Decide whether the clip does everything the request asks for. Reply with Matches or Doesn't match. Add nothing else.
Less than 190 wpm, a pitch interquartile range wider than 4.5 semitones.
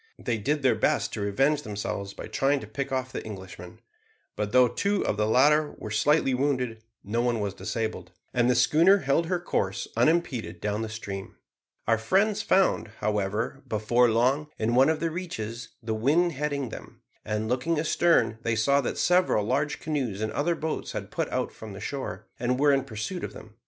Doesn't match